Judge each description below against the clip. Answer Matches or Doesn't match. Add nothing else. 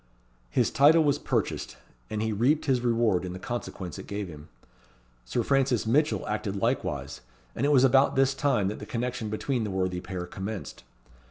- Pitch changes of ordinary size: Doesn't match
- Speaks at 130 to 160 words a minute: Doesn't match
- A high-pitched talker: Doesn't match